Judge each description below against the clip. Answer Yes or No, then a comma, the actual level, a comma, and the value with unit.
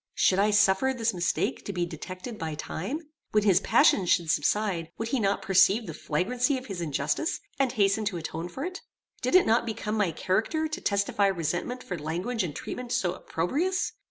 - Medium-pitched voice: No, high, 200 Hz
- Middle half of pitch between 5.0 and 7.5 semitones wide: Yes, wide, 5.6 semitones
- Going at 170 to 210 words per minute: Yes, average, 190 wpm